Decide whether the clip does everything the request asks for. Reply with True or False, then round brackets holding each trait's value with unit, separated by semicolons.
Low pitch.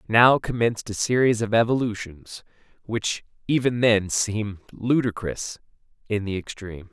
True (110 Hz)